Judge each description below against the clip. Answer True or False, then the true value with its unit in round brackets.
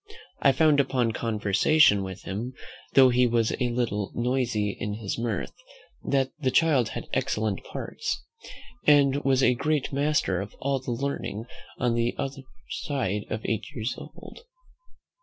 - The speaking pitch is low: True (125 Hz)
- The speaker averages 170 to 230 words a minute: False (145 wpm)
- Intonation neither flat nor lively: True (4.1 semitones)